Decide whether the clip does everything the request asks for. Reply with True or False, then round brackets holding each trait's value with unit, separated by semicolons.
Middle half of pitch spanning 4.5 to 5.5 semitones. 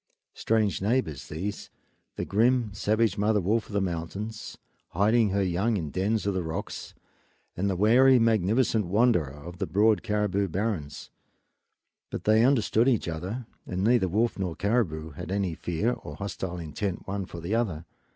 False (4.1 semitones)